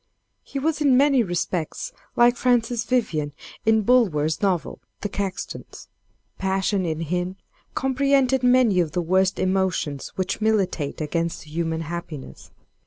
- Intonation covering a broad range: Yes, wide, 6.6 semitones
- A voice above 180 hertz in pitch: Yes, high, 190 Hz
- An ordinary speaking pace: No, slow, 130 wpm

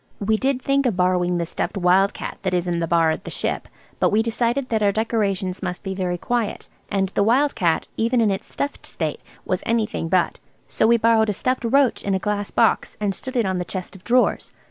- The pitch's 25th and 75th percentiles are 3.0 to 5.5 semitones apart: Yes, average, 4.2 semitones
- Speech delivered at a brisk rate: Yes, fast, 230 wpm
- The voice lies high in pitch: Yes, high, 205 Hz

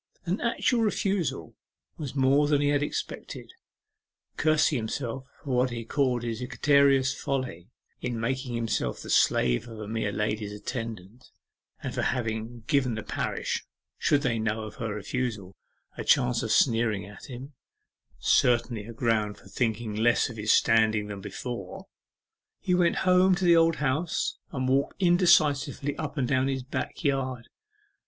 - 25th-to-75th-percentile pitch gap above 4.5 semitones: No, average, 4.2 semitones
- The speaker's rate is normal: Yes, average, 155 wpm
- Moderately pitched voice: No, low, 125 Hz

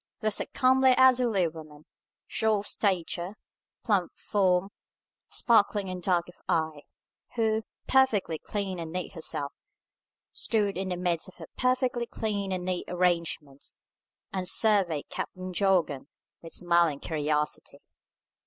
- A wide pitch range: No, average, 4.1 semitones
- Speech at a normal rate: No, slow, 130 wpm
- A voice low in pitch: No, medium, 185 Hz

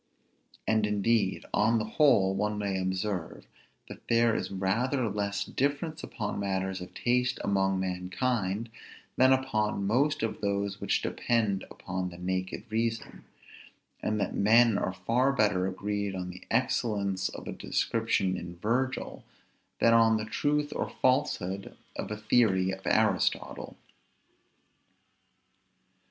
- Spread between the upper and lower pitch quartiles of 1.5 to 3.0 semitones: No, average, 3.5 semitones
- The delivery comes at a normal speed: No, slow, 130 wpm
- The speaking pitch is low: Yes, low, 105 Hz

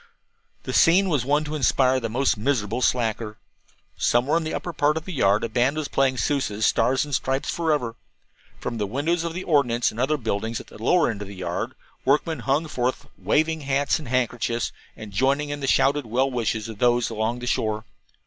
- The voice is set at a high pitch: No, low, 130 Hz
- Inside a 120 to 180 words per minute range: No, fast, 205 wpm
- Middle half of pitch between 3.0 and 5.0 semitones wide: Yes, average, 4.4 semitones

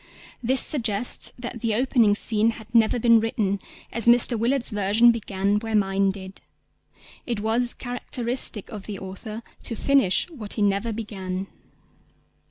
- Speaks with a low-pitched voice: No, high, 220 Hz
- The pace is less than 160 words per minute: Yes, average, 145 wpm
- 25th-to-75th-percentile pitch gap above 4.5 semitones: No, average, 2.8 semitones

